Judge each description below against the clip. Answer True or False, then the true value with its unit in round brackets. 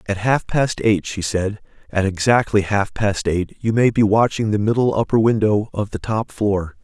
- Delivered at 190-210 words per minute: True (200 wpm)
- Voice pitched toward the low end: True (105 Hz)